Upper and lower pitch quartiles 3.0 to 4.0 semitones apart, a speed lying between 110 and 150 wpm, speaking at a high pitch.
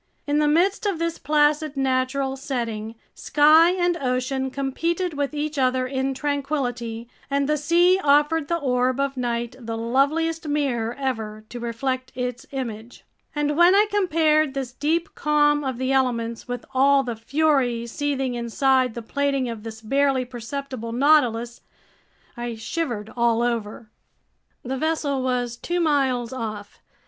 Yes: average, 3.6 semitones; average, 145 wpm; very high, 265 Hz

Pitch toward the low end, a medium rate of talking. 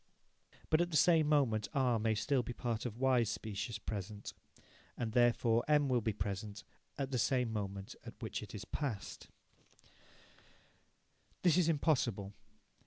Yes: low, 120 Hz; average, 150 wpm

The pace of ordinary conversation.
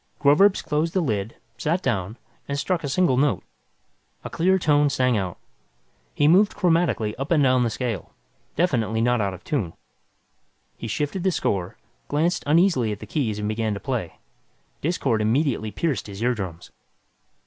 Yes: average, 160 wpm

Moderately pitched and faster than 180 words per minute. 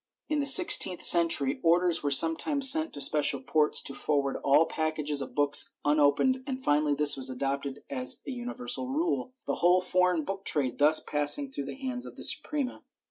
Yes: medium, 165 Hz; average, 190 wpm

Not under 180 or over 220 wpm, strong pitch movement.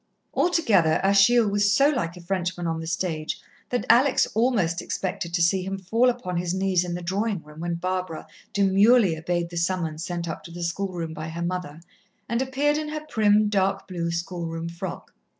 No: average, 185 wpm; average, 3.5 semitones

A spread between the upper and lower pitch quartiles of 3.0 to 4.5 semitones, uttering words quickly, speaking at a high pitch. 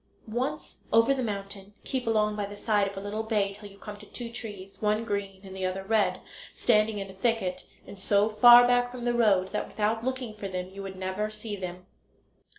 No: narrow, 2.5 semitones; fast, 220 wpm; high, 210 Hz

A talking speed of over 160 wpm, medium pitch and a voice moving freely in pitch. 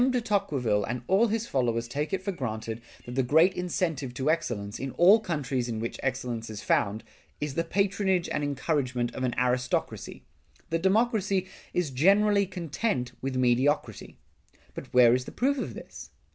Yes: average, 170 wpm; medium, 145 Hz; wide, 7.5 semitones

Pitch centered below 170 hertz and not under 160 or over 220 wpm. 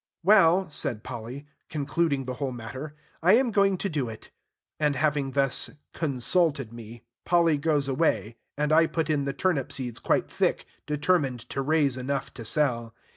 Yes: medium, 140 Hz; average, 165 wpm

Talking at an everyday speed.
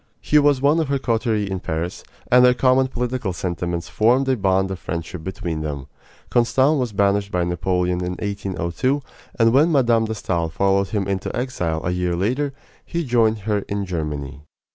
Yes: average, 180 wpm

